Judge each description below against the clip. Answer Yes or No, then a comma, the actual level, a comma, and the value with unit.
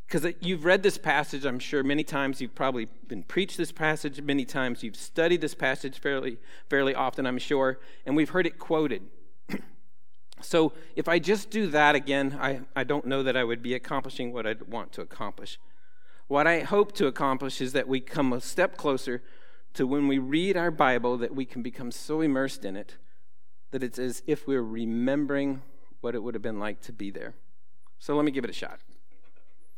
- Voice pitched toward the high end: No, medium, 140 Hz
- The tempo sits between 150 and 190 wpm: No, average, 200 wpm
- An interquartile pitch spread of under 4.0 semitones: Yes, average, 3.1 semitones